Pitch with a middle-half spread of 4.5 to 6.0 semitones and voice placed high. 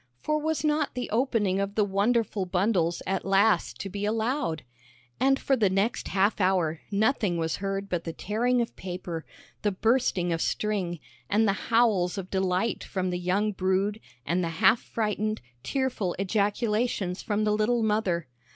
No: average, 3.4 semitones; high, 205 Hz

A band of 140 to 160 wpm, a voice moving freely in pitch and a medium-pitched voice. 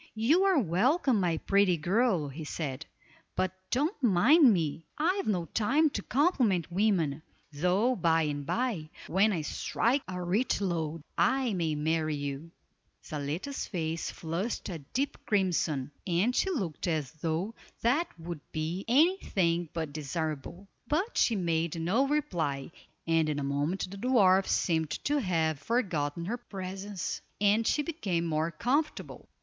Yes: average, 145 wpm; wide, 6.7 semitones; medium, 180 Hz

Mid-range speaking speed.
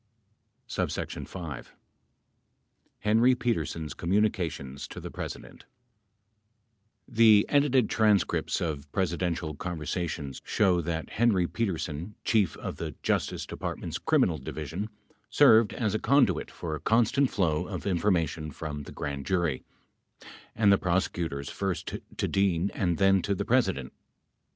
No: slow, 120 wpm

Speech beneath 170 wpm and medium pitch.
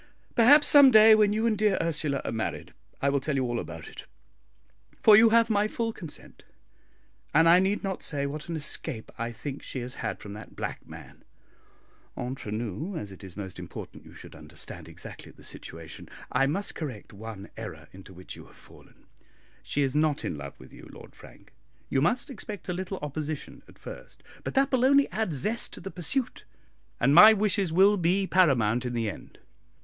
No: average, 195 wpm; medium, 160 Hz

